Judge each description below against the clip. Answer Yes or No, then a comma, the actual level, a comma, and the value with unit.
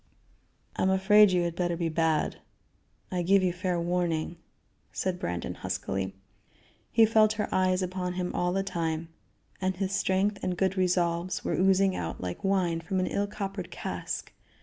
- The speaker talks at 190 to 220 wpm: No, average, 170 wpm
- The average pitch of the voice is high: No, medium, 180 Hz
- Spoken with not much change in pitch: Yes, narrow, 2.2 semitones